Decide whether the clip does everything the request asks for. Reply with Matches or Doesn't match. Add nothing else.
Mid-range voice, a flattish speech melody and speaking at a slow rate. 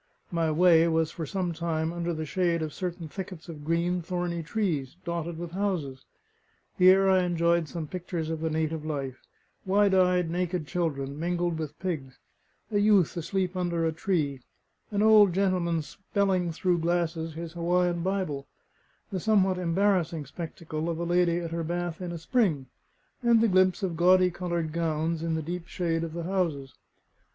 Doesn't match